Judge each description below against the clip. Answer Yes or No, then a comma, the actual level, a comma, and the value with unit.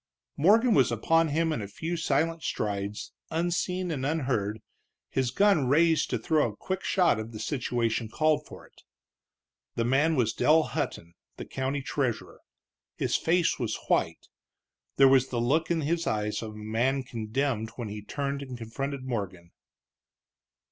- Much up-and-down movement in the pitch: Yes, wide, 6.1 semitones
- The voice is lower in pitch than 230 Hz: Yes, low, 135 Hz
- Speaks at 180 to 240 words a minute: No, average, 160 wpm